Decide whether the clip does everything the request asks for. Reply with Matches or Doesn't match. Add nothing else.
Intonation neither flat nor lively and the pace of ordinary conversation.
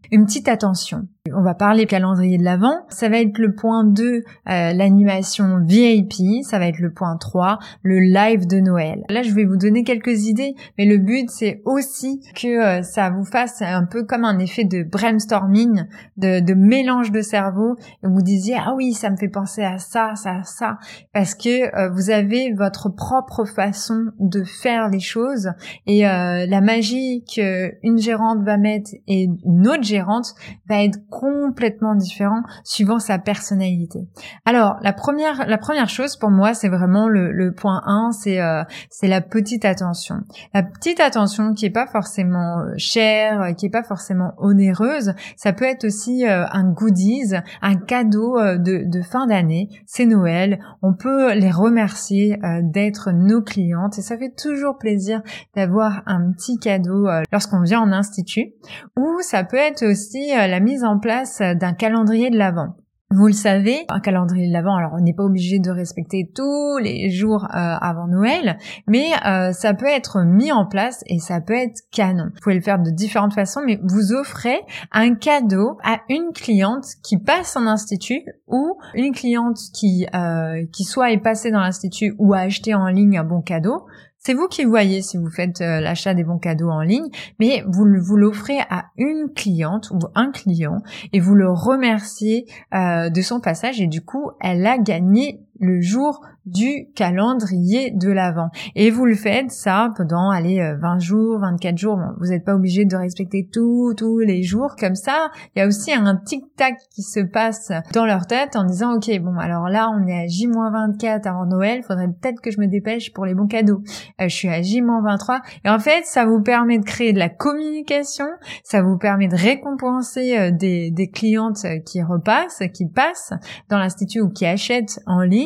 Matches